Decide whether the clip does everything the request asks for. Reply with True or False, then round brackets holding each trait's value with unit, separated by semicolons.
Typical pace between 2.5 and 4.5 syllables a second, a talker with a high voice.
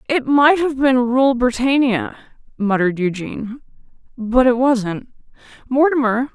True (4.4 syllables/s; 250 Hz)